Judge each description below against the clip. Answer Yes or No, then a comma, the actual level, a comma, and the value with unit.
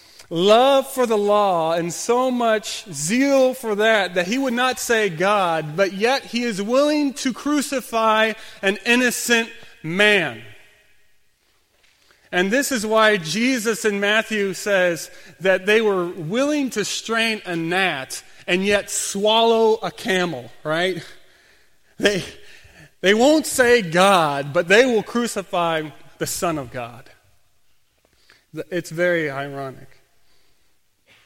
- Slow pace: Yes, slow, 125 wpm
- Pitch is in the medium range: No, high, 205 Hz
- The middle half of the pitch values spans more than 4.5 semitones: Yes, average, 5.1 semitones